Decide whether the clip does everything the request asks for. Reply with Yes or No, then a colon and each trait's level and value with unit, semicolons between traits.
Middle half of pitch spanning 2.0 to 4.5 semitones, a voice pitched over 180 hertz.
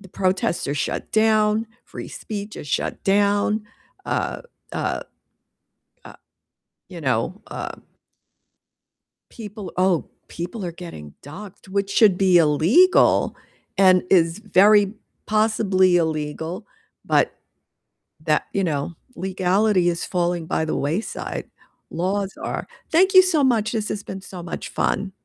Yes: average, 3.6 semitones; high, 190 Hz